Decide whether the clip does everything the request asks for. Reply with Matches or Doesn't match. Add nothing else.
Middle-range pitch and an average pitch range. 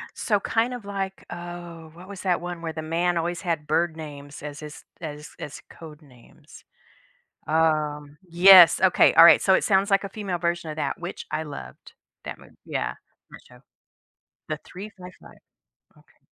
Matches